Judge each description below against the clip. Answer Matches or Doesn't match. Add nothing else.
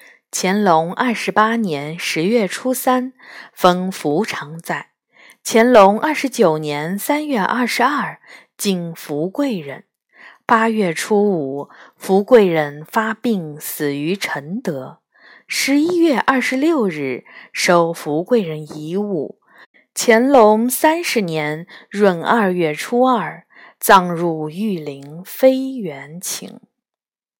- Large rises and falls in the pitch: Matches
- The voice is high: Matches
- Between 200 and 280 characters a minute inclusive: Doesn't match